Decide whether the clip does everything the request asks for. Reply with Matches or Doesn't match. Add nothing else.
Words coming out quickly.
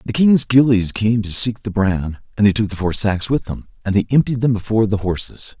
Matches